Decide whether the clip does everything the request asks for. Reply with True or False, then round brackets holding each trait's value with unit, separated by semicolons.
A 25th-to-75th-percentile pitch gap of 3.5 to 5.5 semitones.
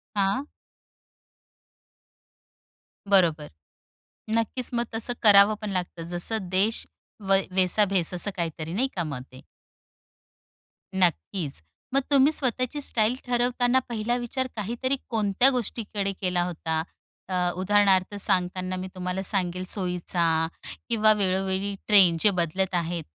True (3.9 semitones)